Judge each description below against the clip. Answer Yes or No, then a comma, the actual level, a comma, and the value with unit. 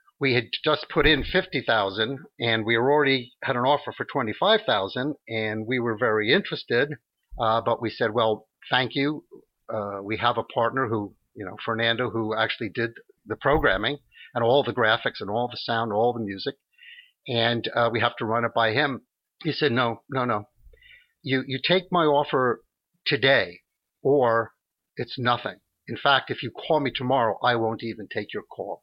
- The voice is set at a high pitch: No, low, 120 Hz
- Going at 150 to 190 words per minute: Yes, average, 185 wpm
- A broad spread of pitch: No, average, 3.6 semitones